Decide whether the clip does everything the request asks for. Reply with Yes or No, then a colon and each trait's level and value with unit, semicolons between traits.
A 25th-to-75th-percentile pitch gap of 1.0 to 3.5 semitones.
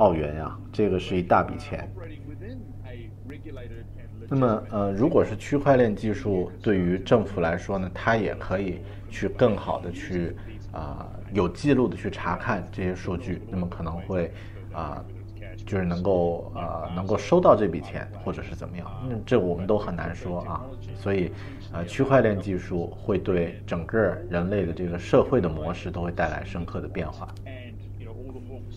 Yes: average, 2.9 semitones